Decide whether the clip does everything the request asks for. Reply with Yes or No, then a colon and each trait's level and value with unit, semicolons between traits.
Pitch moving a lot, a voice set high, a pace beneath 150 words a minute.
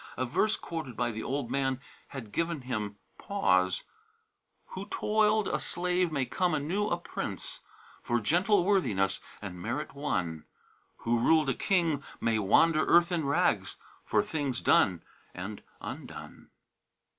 No: wide, 7.3 semitones; medium, 140 Hz; average, 140 wpm